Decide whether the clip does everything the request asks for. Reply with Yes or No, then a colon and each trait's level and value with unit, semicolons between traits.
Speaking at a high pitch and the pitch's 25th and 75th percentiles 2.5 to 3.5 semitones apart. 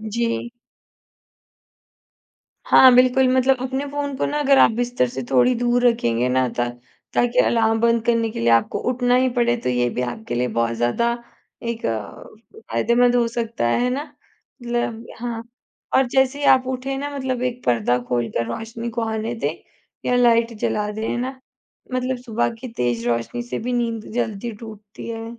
Yes: high, 235 Hz; average, 2.9 semitones